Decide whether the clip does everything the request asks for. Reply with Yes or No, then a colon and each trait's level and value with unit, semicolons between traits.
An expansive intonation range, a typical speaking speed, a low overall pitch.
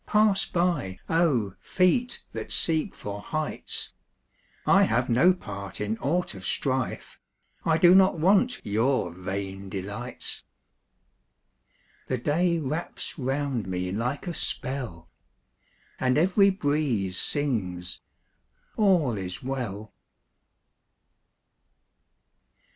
No: wide, 8.9 semitones; slow, 100 wpm; low, 130 Hz